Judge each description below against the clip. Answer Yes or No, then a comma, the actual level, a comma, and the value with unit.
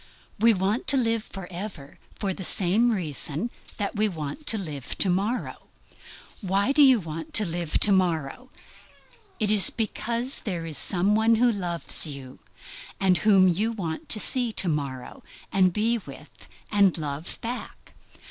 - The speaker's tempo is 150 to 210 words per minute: Yes, average, 155 wpm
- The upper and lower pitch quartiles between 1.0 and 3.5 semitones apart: No, average, 5.1 semitones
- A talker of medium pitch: No, high, 195 Hz